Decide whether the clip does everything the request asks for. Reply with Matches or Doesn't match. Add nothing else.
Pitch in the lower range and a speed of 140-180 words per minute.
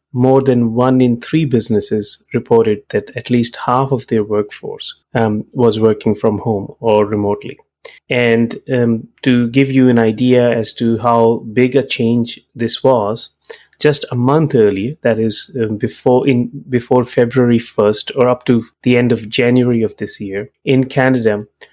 Matches